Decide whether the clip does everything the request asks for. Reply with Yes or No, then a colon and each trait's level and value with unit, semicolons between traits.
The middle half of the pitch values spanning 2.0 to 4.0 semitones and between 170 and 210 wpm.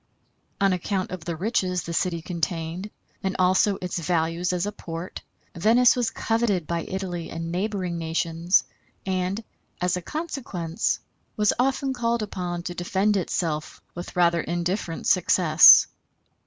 No: average, 2.8 semitones; average, 140 wpm